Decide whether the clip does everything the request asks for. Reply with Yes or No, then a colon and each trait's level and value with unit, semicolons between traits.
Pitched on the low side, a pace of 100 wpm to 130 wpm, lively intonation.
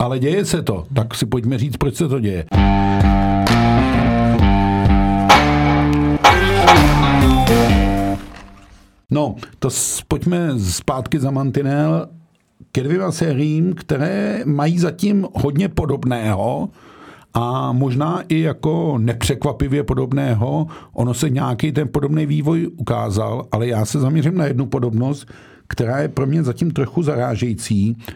Yes: low, 130 Hz; slow, 115 wpm; wide, 5.8 semitones